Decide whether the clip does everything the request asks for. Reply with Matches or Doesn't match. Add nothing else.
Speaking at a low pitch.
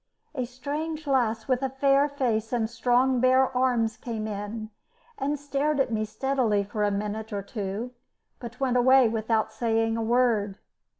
Doesn't match